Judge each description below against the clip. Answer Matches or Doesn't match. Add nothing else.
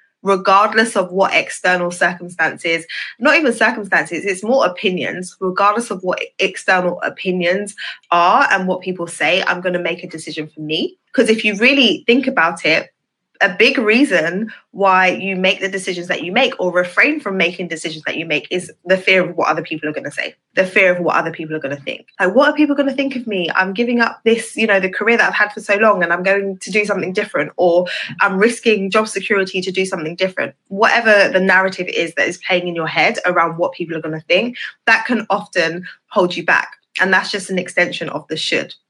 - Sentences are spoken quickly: Matches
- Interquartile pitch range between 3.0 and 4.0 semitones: Matches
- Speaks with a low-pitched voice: Doesn't match